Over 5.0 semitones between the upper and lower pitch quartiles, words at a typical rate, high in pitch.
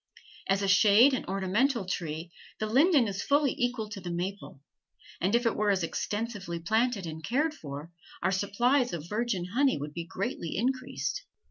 Yes: wide, 5.4 semitones; average, 170 wpm; high, 205 Hz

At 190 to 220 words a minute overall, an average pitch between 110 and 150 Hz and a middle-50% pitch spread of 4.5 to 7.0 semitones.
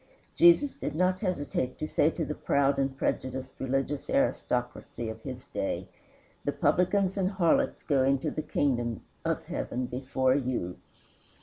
No: average, 145 wpm; low, 135 Hz; average, 4.9 semitones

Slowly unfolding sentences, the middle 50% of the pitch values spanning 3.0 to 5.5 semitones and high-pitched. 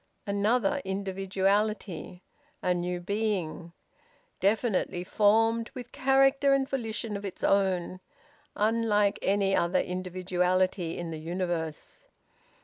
Yes: slow, 100 wpm; average, 3.5 semitones; high, 195 Hz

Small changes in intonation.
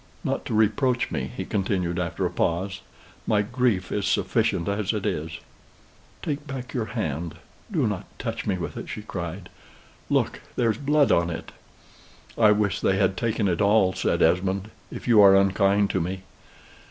No: average, 3.3 semitones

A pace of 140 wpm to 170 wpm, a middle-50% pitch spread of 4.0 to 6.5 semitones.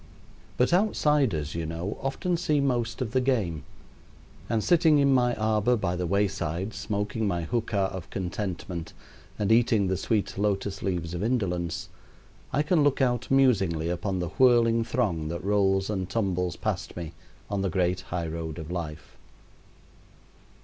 Yes: average, 155 wpm; wide, 5.5 semitones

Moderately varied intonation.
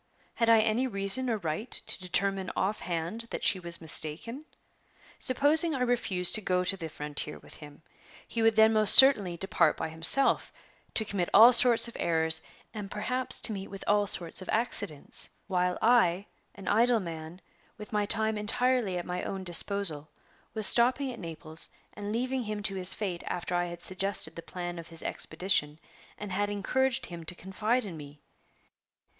Yes: average, 4.6 semitones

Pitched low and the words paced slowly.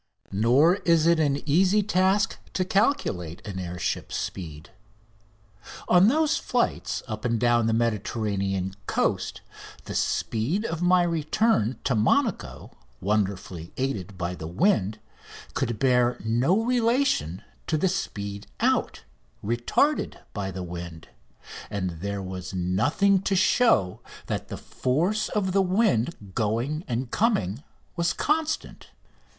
Yes: low, 120 Hz; slow, 125 wpm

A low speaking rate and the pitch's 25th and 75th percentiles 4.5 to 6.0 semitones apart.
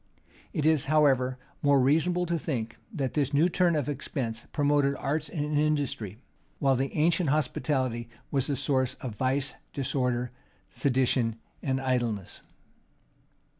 No: slow, 130 wpm; average, 2.9 semitones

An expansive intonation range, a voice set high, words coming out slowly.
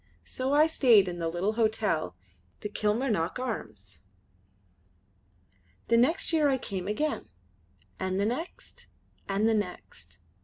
Yes: wide, 5.9 semitones; high, 215 Hz; slow, 125 wpm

